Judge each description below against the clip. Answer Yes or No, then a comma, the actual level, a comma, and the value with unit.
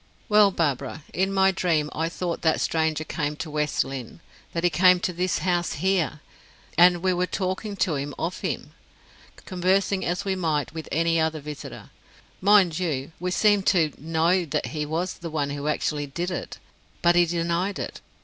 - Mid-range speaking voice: Yes, medium, 170 Hz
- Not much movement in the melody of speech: No, average, 3.1 semitones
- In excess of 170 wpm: Yes, average, 180 wpm